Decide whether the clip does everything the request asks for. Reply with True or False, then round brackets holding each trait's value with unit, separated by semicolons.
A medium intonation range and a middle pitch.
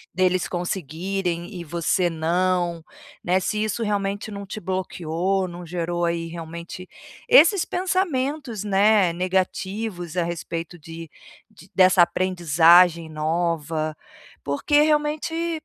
True (3.1 semitones; 180 Hz)